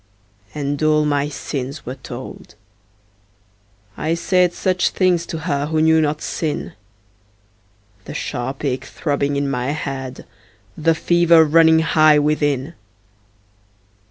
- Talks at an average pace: No, slow, 120 wpm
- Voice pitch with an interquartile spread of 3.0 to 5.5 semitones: No, narrow, 2.4 semitones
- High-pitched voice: No, medium, 150 Hz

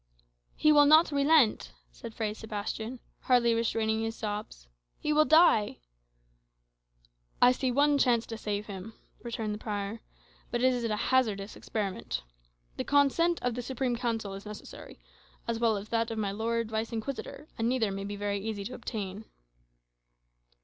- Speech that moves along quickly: No, average, 160 wpm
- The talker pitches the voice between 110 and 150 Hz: No, high, 225 Hz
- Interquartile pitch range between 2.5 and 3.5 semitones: Yes, average, 3.1 semitones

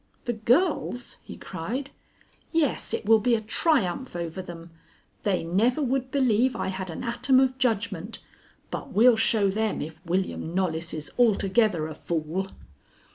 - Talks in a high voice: Yes, high, 215 Hz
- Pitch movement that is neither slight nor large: No, wide, 5.9 semitones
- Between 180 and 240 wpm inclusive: No, average, 150 wpm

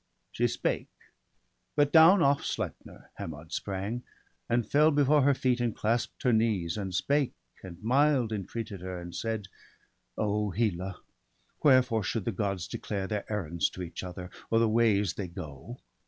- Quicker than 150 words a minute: Yes, average, 165 wpm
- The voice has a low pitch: Yes, low, 105 Hz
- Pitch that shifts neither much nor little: Yes, average, 4.7 semitones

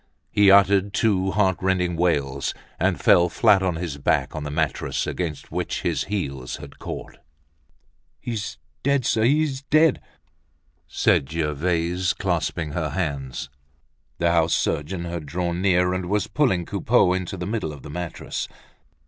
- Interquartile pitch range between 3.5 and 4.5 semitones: Yes, average, 4.0 semitones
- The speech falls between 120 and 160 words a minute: Yes, average, 150 wpm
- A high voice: No, very low, 90 Hz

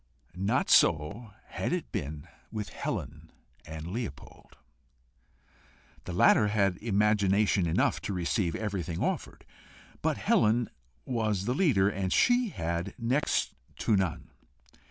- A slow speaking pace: Yes, slow, 115 wpm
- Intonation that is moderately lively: Yes, average, 4.3 semitones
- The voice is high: No, low, 100 Hz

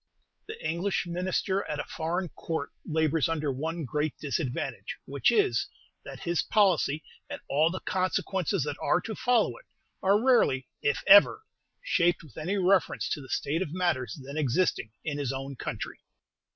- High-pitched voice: No, medium, 165 Hz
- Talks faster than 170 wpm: No, average, 165 wpm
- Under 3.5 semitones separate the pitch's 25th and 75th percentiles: No, average, 4.5 semitones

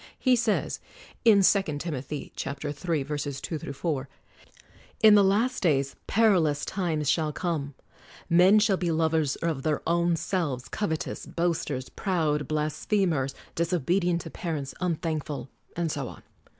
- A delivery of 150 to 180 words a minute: No, slow, 135 wpm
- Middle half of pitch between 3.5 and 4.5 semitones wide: Yes, average, 3.8 semitones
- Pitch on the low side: No, medium, 160 Hz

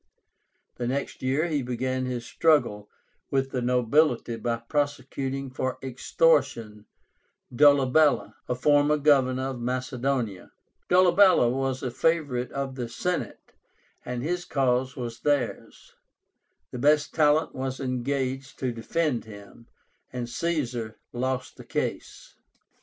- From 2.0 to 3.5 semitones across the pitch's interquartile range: Yes, average, 3.0 semitones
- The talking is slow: Yes, slow, 120 wpm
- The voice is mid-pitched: No, low, 130 Hz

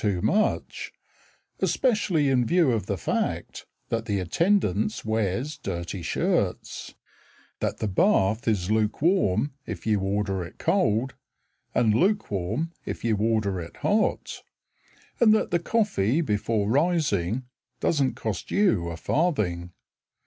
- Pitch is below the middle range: Yes, low, 110 Hz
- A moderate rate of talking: No, slow, 125 wpm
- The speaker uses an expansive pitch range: Yes, wide, 8.9 semitones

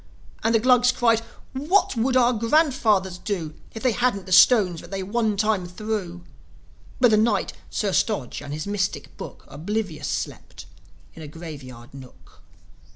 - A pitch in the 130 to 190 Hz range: No, high, 210 Hz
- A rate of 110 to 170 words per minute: Yes, average, 160 wpm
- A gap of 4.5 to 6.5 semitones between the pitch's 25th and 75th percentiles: Yes, average, 5.2 semitones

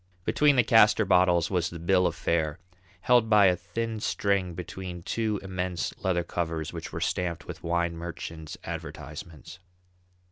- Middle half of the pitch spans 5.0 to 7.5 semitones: No, average, 2.9 semitones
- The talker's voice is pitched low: Yes, very low, 90 Hz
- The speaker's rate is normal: Yes, average, 150 wpm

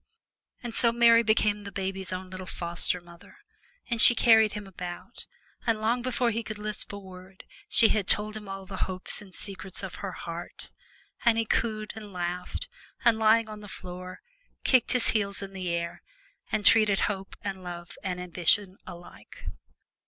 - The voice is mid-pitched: No, high, 200 Hz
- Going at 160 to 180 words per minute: Yes, average, 175 wpm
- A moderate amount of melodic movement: Yes, average, 3.1 semitones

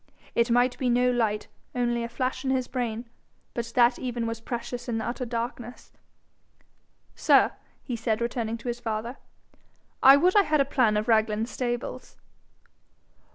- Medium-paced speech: Yes, average, 160 wpm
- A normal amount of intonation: No, narrow, 1.6 semitones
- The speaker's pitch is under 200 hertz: No, high, 240 Hz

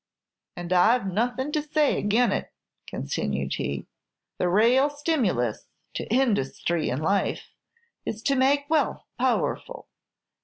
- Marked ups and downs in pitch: Yes, wide, 8.0 semitones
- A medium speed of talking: No, slow, 125 wpm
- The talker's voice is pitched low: No, high, 230 Hz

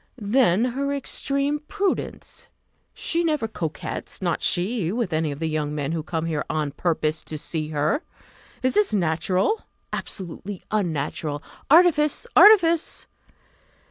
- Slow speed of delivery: Yes, slow, 130 wpm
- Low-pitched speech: No, medium, 185 Hz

